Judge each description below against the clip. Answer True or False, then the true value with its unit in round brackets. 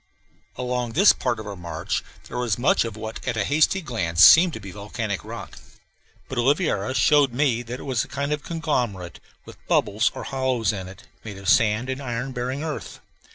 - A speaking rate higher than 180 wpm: True (200 wpm)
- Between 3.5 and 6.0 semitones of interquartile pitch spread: True (4.4 semitones)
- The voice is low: True (120 Hz)